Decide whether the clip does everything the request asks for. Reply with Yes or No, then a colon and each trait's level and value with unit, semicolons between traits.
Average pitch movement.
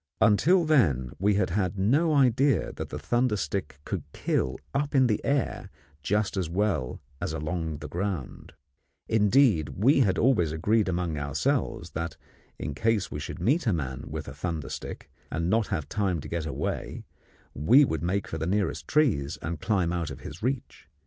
No: wide, 6.4 semitones